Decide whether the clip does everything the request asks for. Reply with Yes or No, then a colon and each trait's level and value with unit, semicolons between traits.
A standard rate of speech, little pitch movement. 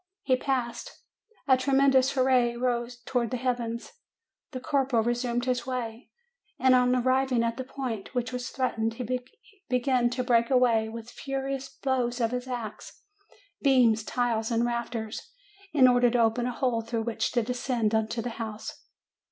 Yes: average, 160 wpm; narrow, 1.8 semitones